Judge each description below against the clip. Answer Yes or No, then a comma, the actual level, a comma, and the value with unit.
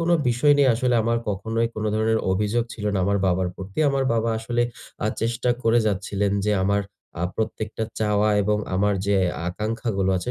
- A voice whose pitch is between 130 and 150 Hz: No, low, 110 Hz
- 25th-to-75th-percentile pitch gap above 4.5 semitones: No, narrow, 2.4 semitones